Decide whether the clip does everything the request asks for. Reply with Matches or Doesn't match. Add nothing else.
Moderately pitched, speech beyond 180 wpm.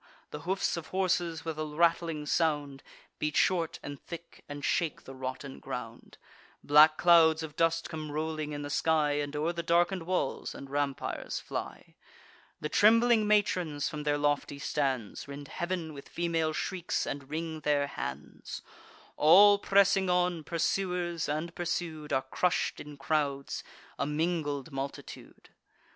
Doesn't match